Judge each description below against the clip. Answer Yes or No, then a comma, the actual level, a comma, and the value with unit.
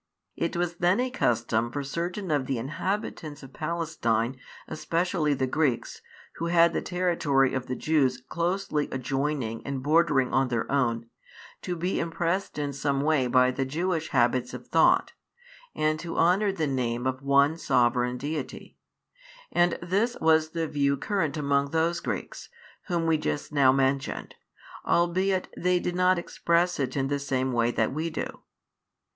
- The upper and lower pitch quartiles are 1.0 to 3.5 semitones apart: No, average, 4.4 semitones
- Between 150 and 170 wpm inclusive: Yes, average, 160 wpm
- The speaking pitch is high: No, medium, 150 Hz